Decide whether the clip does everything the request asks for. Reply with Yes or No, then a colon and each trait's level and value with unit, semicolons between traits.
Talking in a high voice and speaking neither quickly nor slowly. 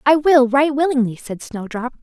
Yes: very high, 265 Hz; average, 180 wpm